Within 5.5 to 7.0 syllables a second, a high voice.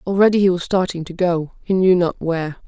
No: 5.7 syllables/s; medium, 180 Hz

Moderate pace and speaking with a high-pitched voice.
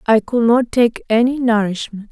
Yes: average, 170 wpm; high, 230 Hz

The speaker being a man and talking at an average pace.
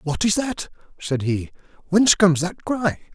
Yes: male; average, 170 wpm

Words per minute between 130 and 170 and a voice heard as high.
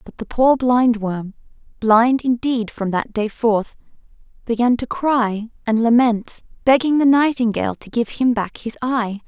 Yes: average, 155 wpm; high, 235 Hz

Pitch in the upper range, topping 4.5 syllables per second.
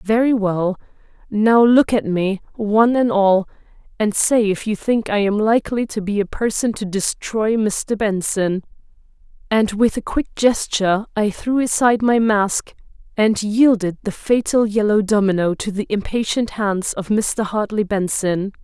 No: high, 210 Hz; 4.4 syllables/s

